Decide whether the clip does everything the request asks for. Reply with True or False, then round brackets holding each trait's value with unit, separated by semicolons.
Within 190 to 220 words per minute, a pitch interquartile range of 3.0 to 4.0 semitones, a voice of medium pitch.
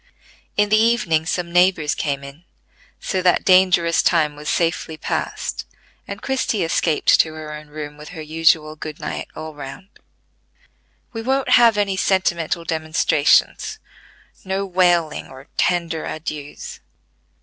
False (140 wpm; 3.5 semitones; 165 Hz)